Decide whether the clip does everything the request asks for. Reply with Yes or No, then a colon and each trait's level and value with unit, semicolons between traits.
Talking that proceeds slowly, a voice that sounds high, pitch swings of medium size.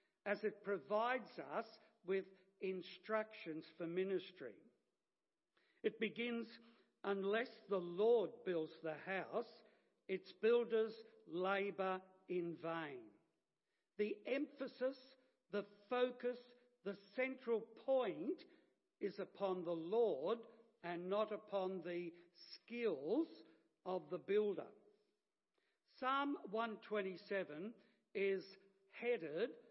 Yes: slow, 90 wpm; high, 205 Hz; average, 4.0 semitones